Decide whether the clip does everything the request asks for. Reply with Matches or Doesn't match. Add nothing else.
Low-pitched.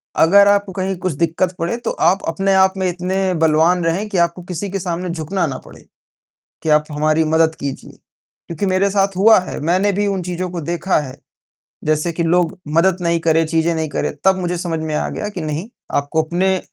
Doesn't match